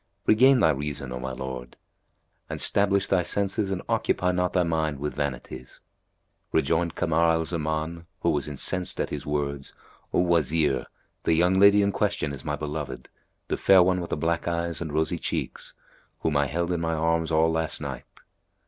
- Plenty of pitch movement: No, average, 3.2 semitones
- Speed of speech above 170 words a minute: Yes, average, 180 wpm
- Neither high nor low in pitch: No, very low, 80 Hz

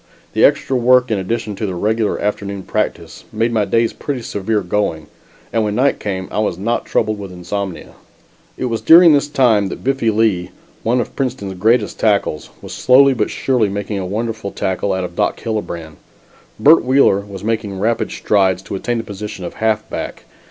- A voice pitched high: No, low, 105 Hz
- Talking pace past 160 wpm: Yes, average, 185 wpm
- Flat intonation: No, average, 3.2 semitones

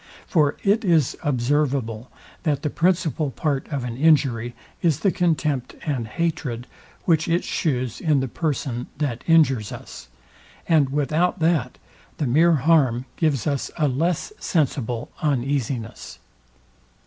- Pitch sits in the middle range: Yes, medium, 145 Hz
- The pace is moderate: No, slow, 130 wpm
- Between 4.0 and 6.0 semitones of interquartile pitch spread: Yes, average, 4.5 semitones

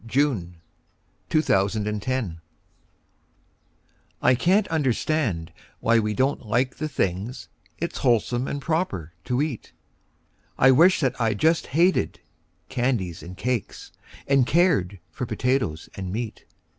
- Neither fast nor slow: No, slow, 125 wpm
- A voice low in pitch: Yes, low, 125 Hz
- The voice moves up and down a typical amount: No, wide, 5.8 semitones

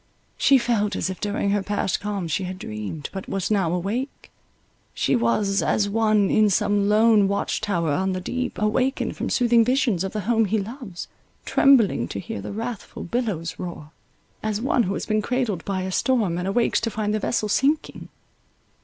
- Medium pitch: No, high, 205 Hz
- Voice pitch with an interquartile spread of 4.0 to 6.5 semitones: No, average, 3.4 semitones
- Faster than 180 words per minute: Yes, average, 190 wpm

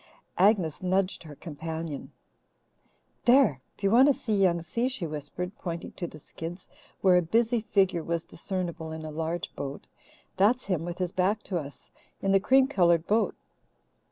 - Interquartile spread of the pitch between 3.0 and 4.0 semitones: Yes, average, 3.7 semitones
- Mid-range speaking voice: Yes, medium, 180 Hz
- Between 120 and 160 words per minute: No, average, 170 wpm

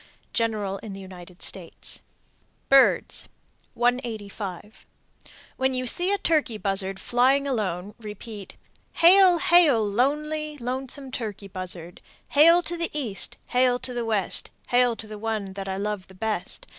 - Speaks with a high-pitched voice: Yes, high, 230 Hz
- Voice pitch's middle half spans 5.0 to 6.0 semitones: Yes, wide, 5.4 semitones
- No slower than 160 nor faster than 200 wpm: No, slow, 135 wpm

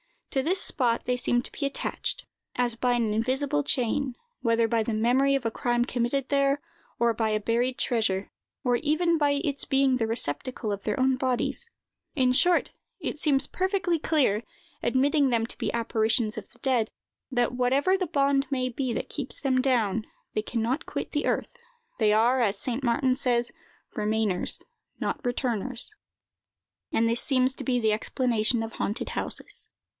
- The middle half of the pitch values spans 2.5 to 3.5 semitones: Yes, average, 3.2 semitones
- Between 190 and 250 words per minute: No, average, 175 wpm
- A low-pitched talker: No, very high, 250 Hz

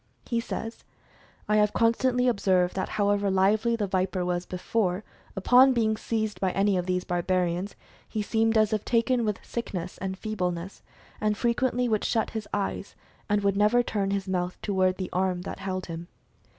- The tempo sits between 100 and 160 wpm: No, average, 175 wpm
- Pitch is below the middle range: No, high, 200 Hz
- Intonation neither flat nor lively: Yes, average, 3.2 semitones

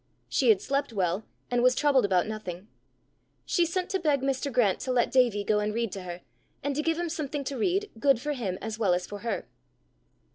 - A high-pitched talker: Yes, high, 245 Hz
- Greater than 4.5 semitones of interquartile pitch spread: Yes, wide, 5.6 semitones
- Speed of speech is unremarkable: No, fast, 220 wpm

